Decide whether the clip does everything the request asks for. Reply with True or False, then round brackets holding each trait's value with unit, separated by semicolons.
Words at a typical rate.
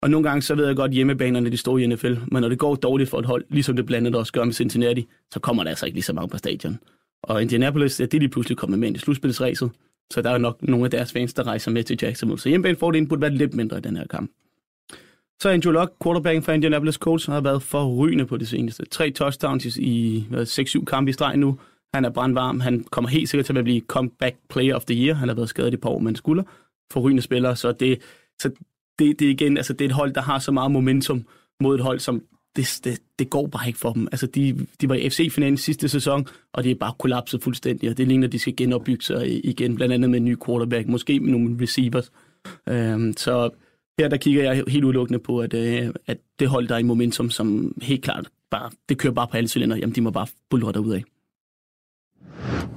False (250 wpm)